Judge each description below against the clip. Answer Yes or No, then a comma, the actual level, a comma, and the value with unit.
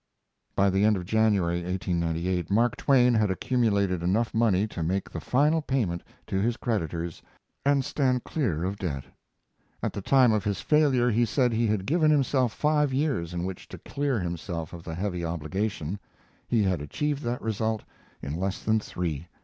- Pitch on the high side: No, low, 105 Hz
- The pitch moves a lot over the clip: Yes, wide, 5.9 semitones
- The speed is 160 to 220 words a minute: Yes, average, 175 wpm